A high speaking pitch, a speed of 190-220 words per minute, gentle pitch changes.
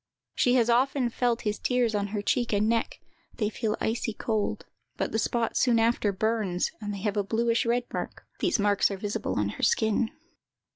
Yes: high, 220 Hz; average, 200 wpm; narrow, 2.3 semitones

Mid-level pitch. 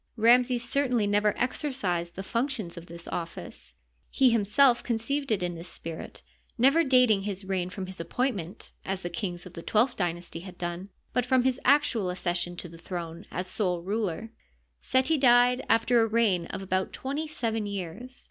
No: high, 205 Hz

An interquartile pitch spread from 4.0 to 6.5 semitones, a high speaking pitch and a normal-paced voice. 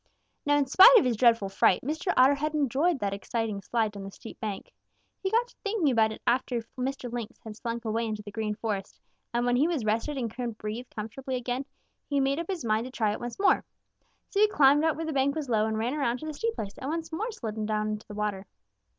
No: average, 5.1 semitones; high, 245 Hz; fast, 245 wpm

